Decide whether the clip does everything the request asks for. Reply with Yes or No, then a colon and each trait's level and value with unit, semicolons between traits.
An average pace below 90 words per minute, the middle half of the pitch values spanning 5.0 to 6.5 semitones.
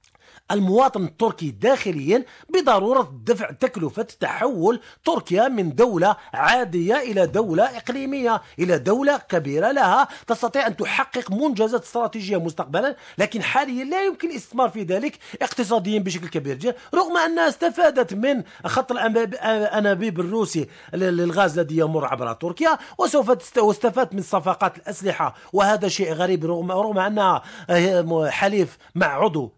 No: average, 125 wpm; wide, 5.6 semitones